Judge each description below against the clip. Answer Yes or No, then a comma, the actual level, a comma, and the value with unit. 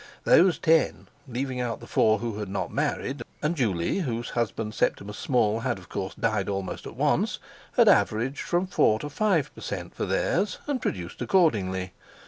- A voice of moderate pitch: No, low, 120 Hz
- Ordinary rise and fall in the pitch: No, wide, 6.6 semitones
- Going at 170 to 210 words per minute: Yes, average, 175 wpm